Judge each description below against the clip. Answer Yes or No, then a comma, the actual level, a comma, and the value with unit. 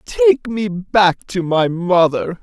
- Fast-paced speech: No, average, 150 wpm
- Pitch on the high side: No, medium, 180 Hz